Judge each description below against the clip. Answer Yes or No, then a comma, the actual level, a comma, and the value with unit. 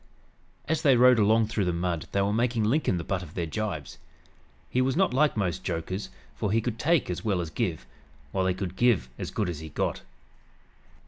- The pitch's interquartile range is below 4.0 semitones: No, wide, 5.4 semitones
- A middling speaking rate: No, fast, 210 wpm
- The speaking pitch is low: Yes, low, 100 Hz